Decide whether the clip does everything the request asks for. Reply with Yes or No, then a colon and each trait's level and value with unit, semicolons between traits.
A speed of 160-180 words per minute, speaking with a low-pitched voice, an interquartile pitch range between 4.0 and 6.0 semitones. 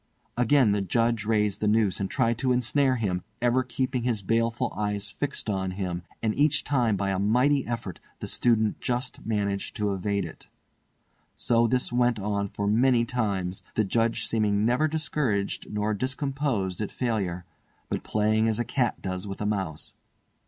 No: average, 170 wpm; low, 110 Hz; average, 3.4 semitones